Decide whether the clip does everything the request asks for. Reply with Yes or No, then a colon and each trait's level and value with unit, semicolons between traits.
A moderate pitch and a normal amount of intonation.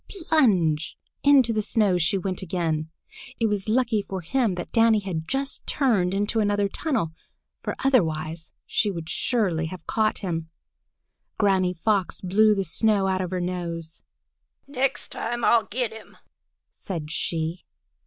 No: high, 195 Hz; average, 4.7 semitones